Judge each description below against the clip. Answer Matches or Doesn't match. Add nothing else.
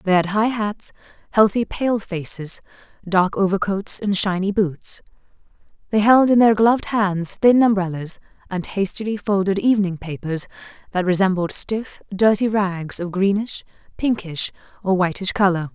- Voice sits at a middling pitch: Doesn't match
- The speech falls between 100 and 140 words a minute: Matches